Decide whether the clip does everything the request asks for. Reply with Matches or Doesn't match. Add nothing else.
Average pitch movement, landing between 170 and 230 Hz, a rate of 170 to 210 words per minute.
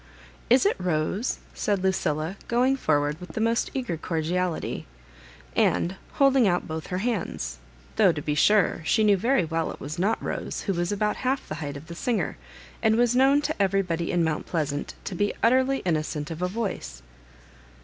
Doesn't match